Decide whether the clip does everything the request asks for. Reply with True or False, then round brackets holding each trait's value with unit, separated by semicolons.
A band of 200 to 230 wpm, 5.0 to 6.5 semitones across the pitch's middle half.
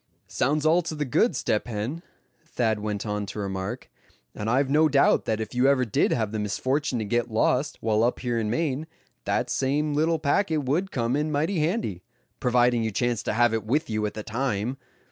True (205 wpm; 5.3 semitones)